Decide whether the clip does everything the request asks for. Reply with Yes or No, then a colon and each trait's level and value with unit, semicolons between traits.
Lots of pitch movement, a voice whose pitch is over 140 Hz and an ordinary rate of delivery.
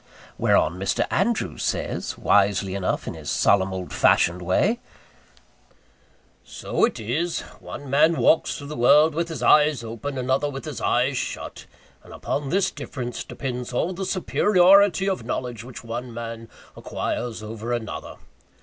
No: wide, 6.1 semitones; low, 125 Hz; average, 150 wpm